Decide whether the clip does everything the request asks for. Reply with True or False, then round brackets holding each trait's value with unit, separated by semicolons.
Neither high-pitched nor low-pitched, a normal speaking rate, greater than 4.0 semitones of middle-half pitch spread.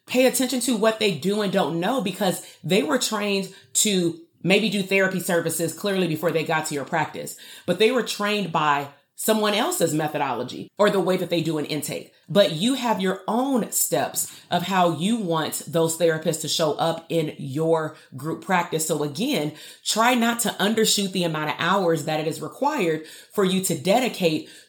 True (180 Hz; 190 wpm; 4.4 semitones)